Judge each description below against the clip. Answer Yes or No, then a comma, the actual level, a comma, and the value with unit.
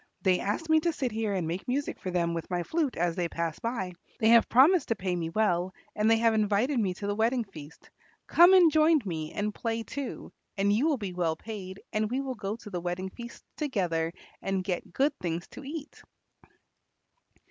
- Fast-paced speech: Yes, fast, 210 wpm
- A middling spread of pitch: No, wide, 6.0 semitones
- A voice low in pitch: No, high, 210 Hz